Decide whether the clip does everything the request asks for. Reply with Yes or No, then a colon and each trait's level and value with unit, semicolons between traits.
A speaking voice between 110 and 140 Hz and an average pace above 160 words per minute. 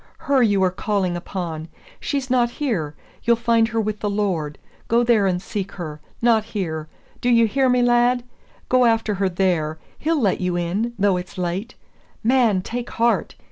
No: high, 210 Hz; average, 180 wpm